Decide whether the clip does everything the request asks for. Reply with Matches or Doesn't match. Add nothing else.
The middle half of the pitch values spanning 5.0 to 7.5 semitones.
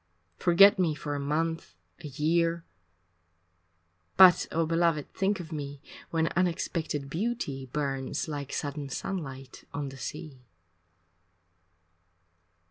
Doesn't match